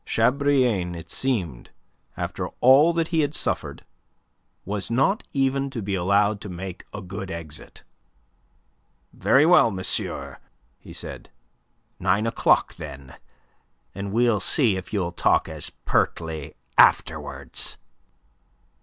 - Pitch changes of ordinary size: No, wide, 6.8 semitones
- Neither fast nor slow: No, slow, 120 wpm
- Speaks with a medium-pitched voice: No, low, 105 Hz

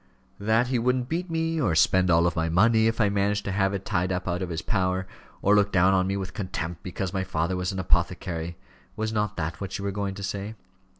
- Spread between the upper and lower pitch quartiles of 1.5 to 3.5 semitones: Yes, average, 2.7 semitones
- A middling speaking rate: No, fast, 240 wpm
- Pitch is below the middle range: Yes, very low, 95 Hz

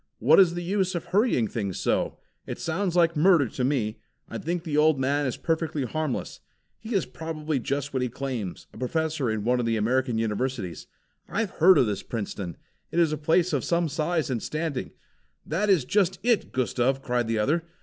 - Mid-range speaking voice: Yes, medium, 145 Hz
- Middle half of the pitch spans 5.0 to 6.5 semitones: Yes, wide, 5.5 semitones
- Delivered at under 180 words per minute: No, average, 200 wpm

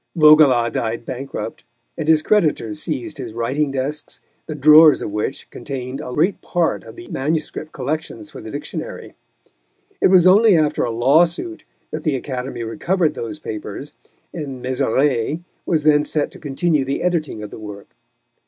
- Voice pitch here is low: No, medium, 150 Hz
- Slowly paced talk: No, average, 160 wpm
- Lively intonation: No, average, 4.1 semitones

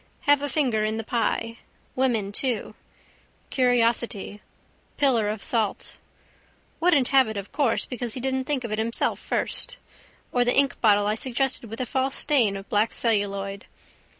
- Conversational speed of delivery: Yes, average, 155 wpm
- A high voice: Yes, high, 235 Hz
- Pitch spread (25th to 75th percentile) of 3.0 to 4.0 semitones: Yes, average, 3.6 semitones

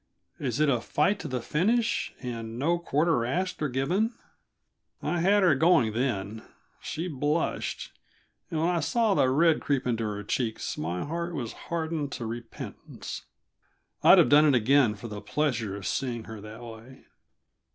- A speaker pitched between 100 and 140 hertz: Yes, low, 135 Hz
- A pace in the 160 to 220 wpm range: Yes, average, 165 wpm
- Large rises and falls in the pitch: Yes, wide, 6.3 semitones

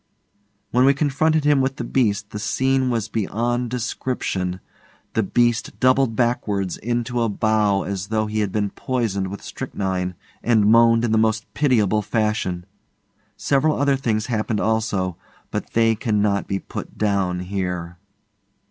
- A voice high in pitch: No, low, 110 Hz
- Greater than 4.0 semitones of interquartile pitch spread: No, average, 3.4 semitones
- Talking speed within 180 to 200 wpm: No, average, 150 wpm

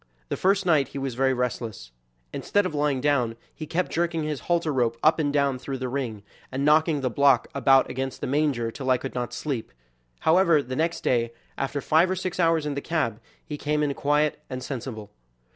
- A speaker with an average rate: No, fast, 210 wpm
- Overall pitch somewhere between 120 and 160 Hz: Yes, medium, 140 Hz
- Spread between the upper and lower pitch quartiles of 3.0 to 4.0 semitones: Yes, average, 3.4 semitones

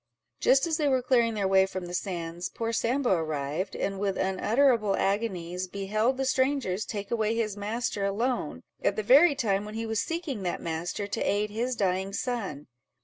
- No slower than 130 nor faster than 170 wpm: No, average, 185 wpm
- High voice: Yes, high, 210 Hz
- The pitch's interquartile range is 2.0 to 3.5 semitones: No, average, 4.1 semitones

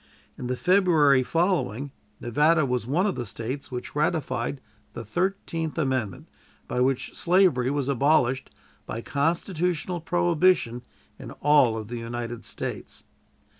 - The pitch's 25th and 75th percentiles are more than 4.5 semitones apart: Yes, wide, 5.5 semitones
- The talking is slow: Yes, slow, 130 wpm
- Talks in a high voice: No, medium, 140 Hz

